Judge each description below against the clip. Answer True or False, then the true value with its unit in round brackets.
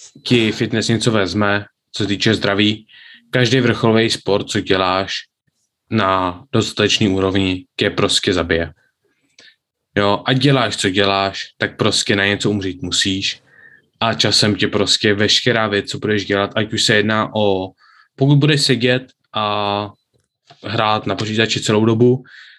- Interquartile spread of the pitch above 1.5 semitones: True (2.6 semitones)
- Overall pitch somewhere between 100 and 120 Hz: True (105 Hz)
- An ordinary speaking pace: True (140 wpm)